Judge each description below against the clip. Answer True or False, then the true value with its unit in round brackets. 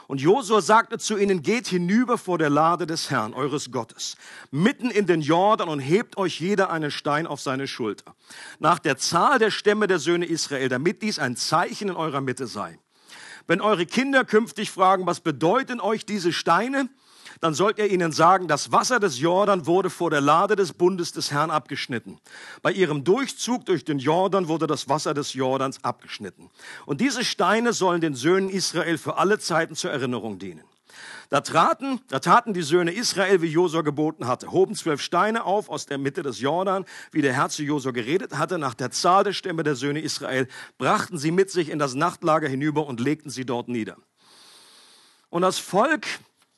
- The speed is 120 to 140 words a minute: False (190 wpm)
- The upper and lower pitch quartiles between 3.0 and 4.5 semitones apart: False (5.2 semitones)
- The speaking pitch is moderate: True (170 Hz)